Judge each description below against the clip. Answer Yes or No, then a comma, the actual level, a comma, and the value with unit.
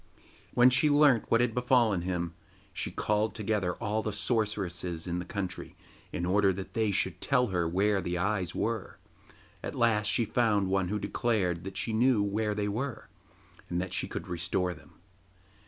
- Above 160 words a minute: Yes, average, 175 wpm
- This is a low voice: Yes, low, 105 Hz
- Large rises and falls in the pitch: No, average, 3.7 semitones